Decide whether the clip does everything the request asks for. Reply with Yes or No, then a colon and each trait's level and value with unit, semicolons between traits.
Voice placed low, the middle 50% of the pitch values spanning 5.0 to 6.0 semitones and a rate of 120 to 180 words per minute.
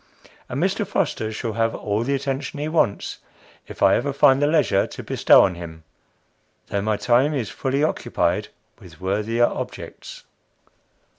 Yes: low, 125 Hz; average, 5.3 semitones; average, 155 wpm